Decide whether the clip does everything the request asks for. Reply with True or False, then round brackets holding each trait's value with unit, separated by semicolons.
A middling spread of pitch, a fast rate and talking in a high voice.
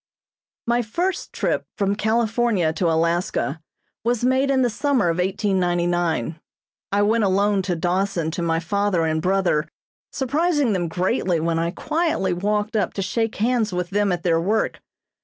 False (4.6 semitones; 160 wpm; 195 Hz)